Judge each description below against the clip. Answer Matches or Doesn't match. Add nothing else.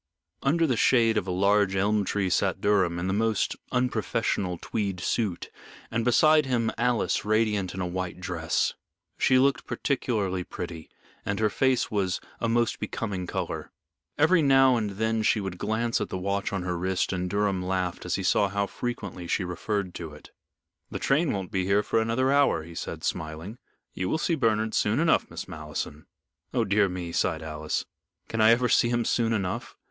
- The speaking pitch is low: Matches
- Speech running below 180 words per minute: Doesn't match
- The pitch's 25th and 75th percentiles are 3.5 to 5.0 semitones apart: Matches